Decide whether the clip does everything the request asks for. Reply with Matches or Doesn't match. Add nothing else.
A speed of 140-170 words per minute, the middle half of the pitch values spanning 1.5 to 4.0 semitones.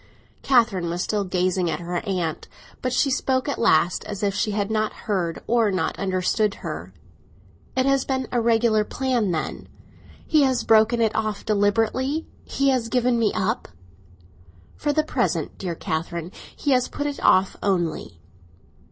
Doesn't match